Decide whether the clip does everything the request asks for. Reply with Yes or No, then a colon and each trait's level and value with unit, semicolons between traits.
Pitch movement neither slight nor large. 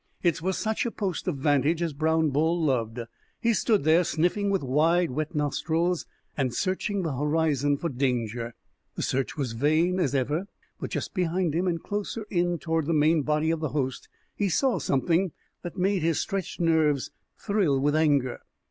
Yes: average, 3.8 semitones